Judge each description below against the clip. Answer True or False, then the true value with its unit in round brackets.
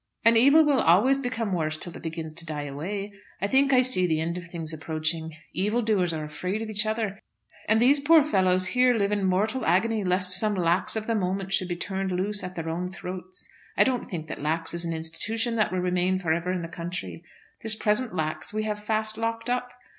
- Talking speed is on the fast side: True (225 wpm)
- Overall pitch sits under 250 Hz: True (190 Hz)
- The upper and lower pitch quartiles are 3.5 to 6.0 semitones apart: True (4.6 semitones)